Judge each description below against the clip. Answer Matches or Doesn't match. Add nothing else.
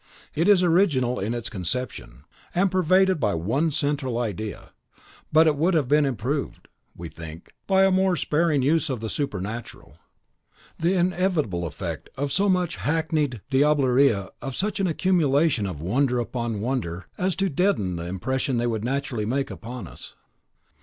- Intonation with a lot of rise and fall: Matches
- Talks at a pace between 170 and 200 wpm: Doesn't match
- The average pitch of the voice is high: Doesn't match